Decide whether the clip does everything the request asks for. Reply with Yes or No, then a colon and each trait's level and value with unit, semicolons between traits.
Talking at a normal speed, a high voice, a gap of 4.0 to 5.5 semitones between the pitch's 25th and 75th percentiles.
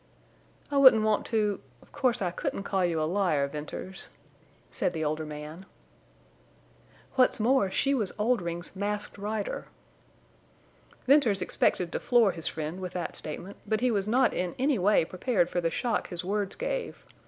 Yes: average, 160 wpm; high, 195 Hz; average, 4.7 semitones